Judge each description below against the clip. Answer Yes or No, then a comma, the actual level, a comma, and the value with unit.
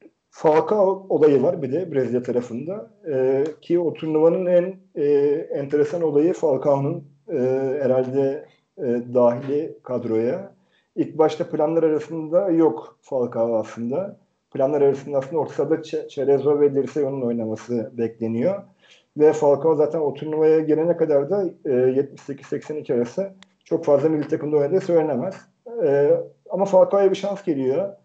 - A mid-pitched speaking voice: Yes, medium, 150 Hz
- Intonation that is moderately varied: Yes, average, 4.8 semitones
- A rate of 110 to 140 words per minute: Yes, average, 130 wpm